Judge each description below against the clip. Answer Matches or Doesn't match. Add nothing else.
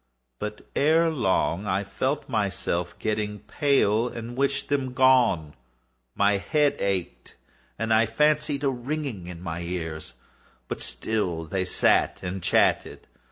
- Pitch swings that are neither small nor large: Doesn't match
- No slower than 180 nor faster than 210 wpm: Doesn't match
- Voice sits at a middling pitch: Doesn't match